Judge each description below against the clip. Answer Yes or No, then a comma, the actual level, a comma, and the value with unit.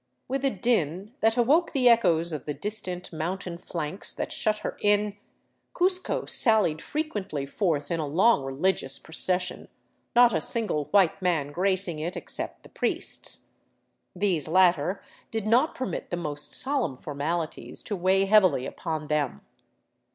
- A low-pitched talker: No, medium, 185 Hz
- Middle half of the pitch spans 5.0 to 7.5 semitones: Yes, wide, 5.6 semitones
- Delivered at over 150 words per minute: No, average, 145 wpm